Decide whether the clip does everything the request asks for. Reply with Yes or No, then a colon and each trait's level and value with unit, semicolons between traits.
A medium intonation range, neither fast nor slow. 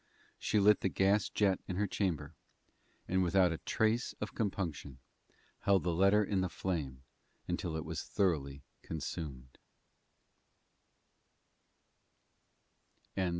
No: average, 3.9 semitones; slow, 110 wpm